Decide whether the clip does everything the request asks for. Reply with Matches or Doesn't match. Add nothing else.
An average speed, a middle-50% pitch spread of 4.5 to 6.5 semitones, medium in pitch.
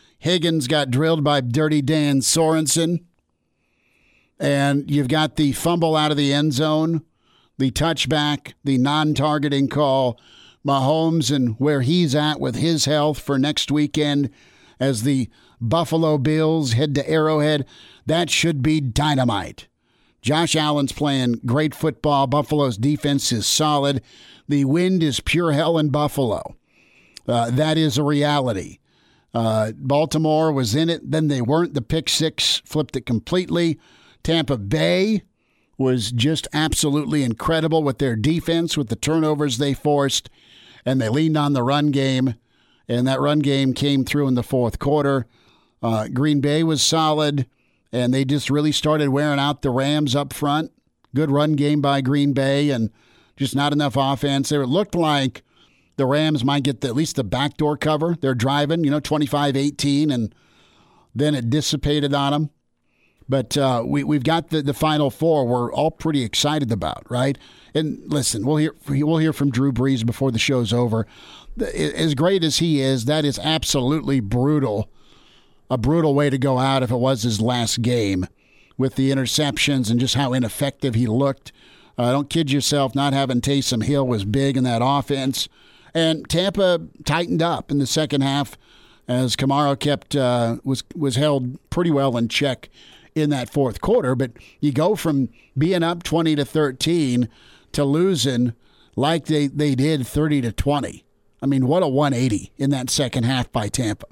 Doesn't match